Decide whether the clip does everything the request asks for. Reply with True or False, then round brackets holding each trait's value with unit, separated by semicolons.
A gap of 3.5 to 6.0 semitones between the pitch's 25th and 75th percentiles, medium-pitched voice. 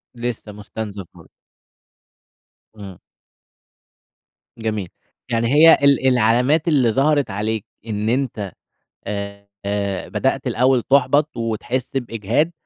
False (4.2 semitones; 115 Hz)